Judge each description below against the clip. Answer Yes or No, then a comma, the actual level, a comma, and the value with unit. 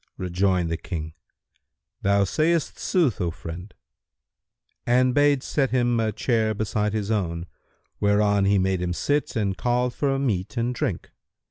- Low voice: Yes, low, 105 Hz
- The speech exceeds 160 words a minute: No, average, 145 wpm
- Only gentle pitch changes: No, average, 5.0 semitones